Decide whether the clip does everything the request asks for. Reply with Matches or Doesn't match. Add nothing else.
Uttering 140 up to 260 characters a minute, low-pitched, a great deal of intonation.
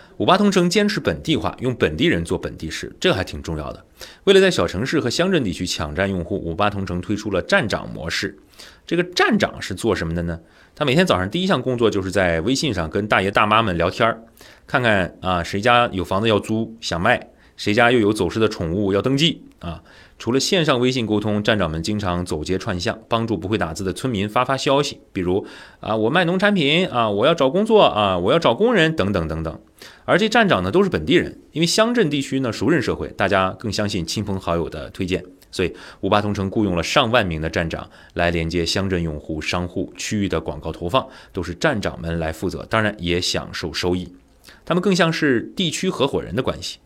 Doesn't match